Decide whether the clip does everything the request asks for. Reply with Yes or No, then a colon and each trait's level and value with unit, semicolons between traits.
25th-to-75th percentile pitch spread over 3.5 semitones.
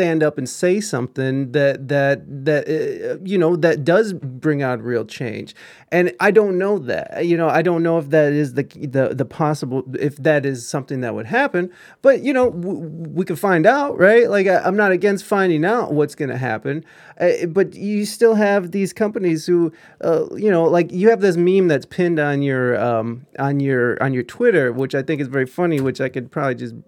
Yes: wide, 5.5 semitones